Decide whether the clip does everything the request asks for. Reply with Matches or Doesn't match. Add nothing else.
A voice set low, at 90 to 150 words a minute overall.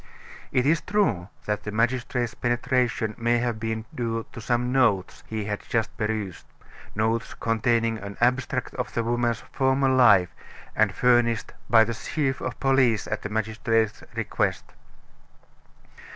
Matches